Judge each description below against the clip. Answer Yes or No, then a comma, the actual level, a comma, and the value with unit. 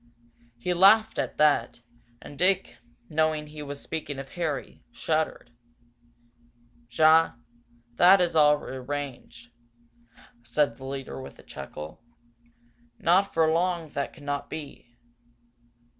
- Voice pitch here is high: No, medium, 150 Hz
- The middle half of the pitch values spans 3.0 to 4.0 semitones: Yes, average, 3.5 semitones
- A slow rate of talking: Yes, slow, 115 wpm